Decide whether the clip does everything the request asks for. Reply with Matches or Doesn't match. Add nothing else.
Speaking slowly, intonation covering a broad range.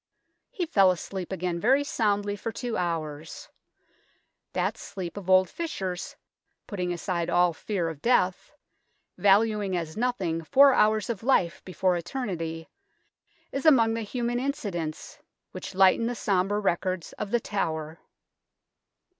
Doesn't match